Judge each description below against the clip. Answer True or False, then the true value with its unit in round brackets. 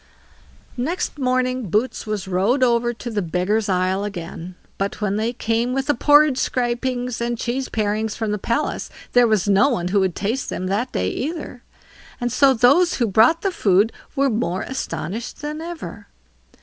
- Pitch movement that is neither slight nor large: True (4.2 semitones)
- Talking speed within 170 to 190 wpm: True (175 wpm)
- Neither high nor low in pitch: False (235 Hz)